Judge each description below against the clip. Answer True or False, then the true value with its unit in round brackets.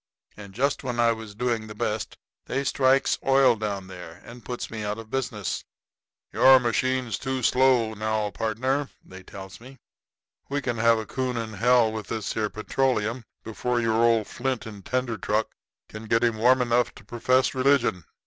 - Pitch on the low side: True (115 Hz)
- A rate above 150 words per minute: True (175 wpm)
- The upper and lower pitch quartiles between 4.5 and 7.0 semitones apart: False (2.9 semitones)